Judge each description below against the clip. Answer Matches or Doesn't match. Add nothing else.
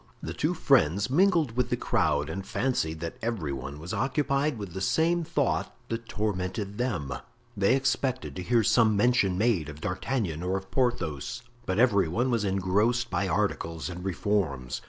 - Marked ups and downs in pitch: Matches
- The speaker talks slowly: Doesn't match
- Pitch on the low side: Matches